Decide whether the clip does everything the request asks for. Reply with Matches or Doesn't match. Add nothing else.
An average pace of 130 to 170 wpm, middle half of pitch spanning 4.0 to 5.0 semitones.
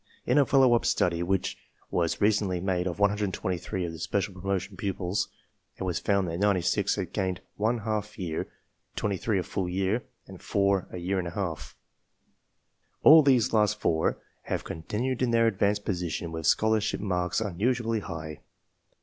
Doesn't match